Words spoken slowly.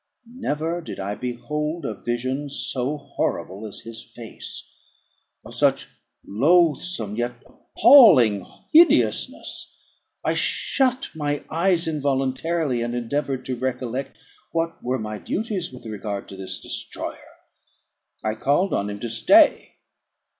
Yes: slow, 120 wpm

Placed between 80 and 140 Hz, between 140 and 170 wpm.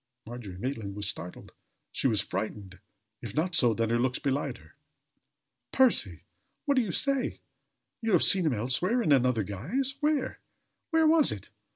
Yes: low, 135 Hz; average, 165 wpm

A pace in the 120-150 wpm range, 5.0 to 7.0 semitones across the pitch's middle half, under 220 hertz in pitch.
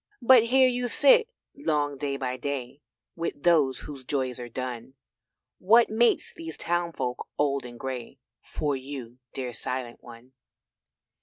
Yes: average, 140 wpm; average, 5.3 semitones; medium, 140 Hz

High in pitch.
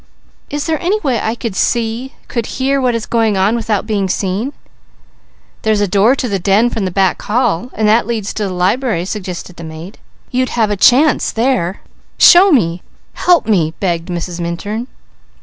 Yes: high, 215 Hz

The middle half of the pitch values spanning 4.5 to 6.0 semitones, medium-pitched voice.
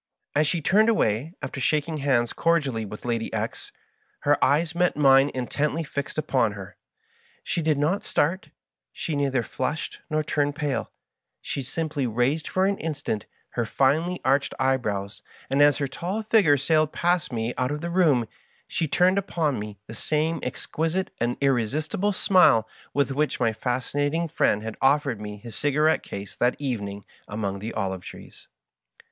Yes: average, 4.9 semitones; medium, 145 Hz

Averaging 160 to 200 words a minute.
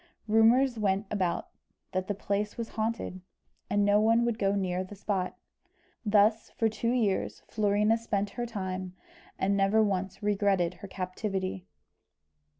No: average, 145 wpm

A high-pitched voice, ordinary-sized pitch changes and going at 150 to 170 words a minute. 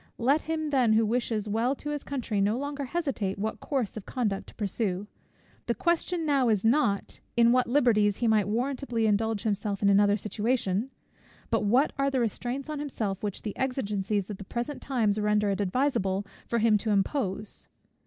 No: high, 225 Hz; average, 4.4 semitones; average, 185 wpm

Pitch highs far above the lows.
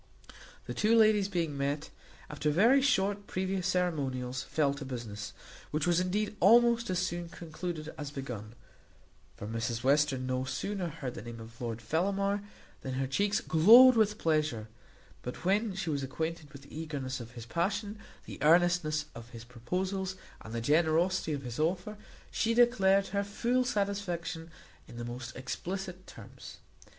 Yes: wide, 6.9 semitones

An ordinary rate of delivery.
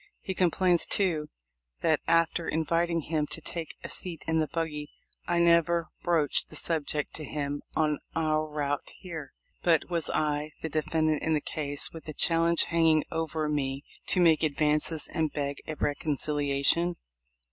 Yes: average, 160 wpm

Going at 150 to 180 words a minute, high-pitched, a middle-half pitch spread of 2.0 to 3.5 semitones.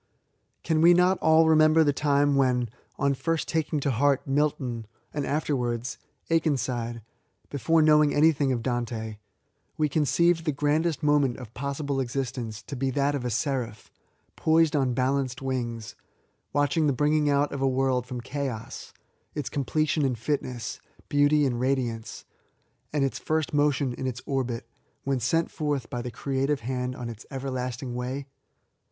No: average, 160 wpm; low, 135 Hz; average, 3.1 semitones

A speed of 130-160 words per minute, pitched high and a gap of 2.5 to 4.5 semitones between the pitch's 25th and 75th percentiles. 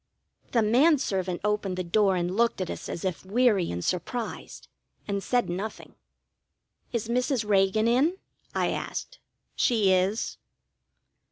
Yes: average, 140 wpm; high, 210 Hz; average, 4.0 semitones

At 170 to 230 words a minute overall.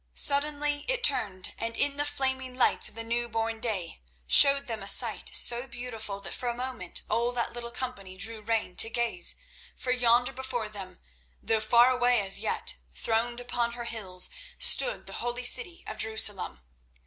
Yes: average, 175 wpm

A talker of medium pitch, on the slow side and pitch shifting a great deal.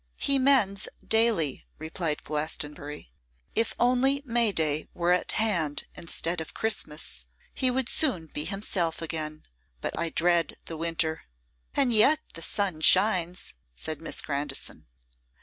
Yes: medium, 170 Hz; slow, 130 wpm; wide, 6.0 semitones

